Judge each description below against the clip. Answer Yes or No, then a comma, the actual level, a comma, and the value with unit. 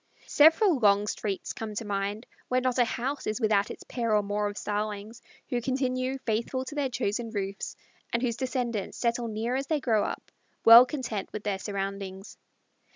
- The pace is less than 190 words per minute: Yes, average, 180 wpm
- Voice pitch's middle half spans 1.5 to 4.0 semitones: Yes, average, 3.7 semitones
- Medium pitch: No, high, 230 Hz